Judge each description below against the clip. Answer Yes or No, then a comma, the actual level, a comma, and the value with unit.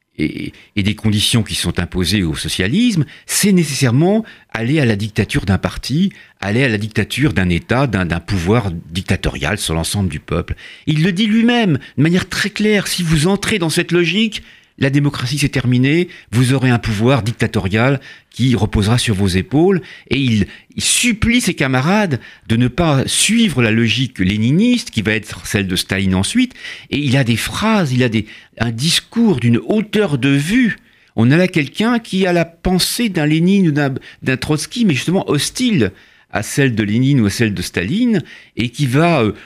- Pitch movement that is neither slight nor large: No, wide, 8.7 semitones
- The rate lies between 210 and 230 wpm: No, average, 185 wpm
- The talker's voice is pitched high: No, low, 135 Hz